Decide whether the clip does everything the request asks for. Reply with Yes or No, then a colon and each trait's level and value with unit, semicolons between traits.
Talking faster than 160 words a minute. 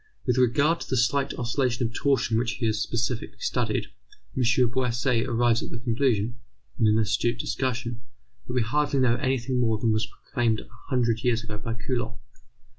Yes: average, 180 wpm